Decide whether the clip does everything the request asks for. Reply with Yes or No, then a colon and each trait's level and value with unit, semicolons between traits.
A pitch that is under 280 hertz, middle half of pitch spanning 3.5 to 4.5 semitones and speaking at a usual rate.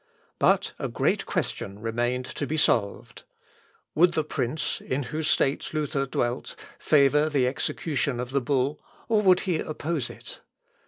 Yes: medium, 140 Hz; average, 3.8 semitones; average, 150 wpm